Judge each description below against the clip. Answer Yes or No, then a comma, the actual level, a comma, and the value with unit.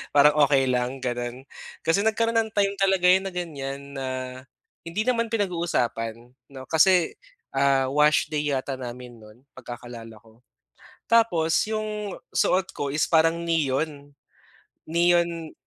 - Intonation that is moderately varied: No, wide, 5.8 semitones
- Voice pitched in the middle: Yes, medium, 155 Hz